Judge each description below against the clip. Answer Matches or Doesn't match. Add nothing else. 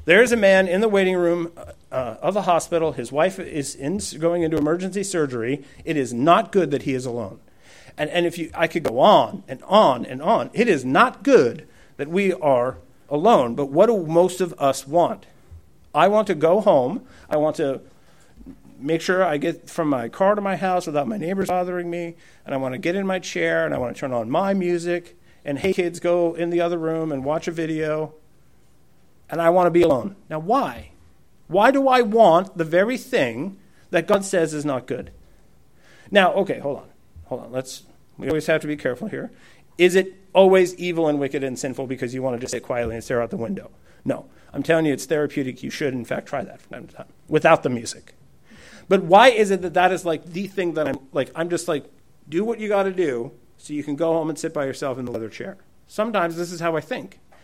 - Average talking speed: Doesn't match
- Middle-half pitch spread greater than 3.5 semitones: Matches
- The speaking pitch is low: Doesn't match